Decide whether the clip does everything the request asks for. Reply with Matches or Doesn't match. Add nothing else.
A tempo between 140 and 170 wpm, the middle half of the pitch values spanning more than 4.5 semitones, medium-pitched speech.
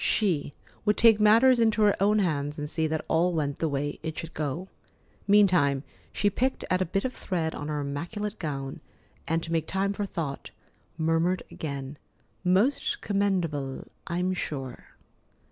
Matches